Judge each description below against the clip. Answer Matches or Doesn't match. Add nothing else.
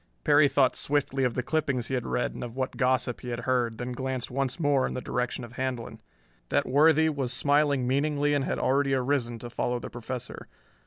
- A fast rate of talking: Matches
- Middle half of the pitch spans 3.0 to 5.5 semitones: Doesn't match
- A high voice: Doesn't match